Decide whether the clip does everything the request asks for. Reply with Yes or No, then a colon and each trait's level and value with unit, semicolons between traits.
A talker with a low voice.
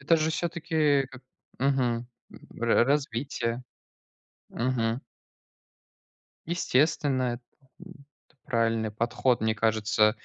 Yes: low, 125 Hz